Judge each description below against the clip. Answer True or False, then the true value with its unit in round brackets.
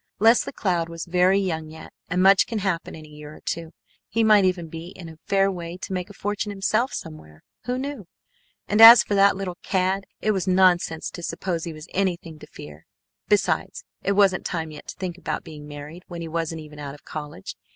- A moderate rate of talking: False (215 wpm)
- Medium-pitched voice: True (180 Hz)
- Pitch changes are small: False (3.5 semitones)